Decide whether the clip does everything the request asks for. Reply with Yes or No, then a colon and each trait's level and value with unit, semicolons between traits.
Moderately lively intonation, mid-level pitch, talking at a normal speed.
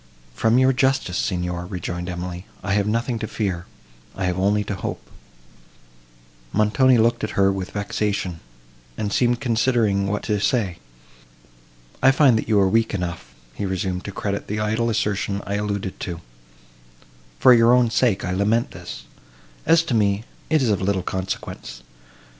No: average, 3.6 semitones; low, 100 Hz; average, 160 wpm